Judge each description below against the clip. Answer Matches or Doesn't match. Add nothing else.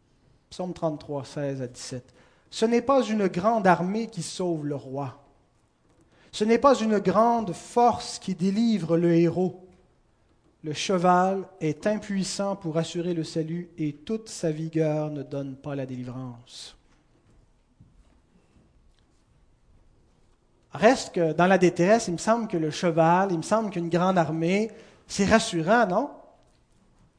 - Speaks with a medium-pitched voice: Matches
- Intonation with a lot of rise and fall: Doesn't match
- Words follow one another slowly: Matches